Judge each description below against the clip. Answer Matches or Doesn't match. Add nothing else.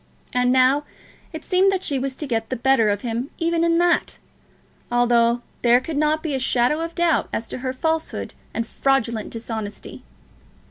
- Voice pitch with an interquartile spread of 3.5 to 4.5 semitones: Doesn't match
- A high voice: Matches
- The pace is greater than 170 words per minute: Matches